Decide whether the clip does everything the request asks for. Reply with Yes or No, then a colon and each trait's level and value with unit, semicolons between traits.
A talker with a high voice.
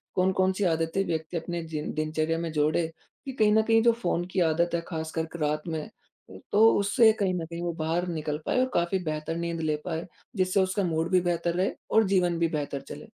No: medium, 170 Hz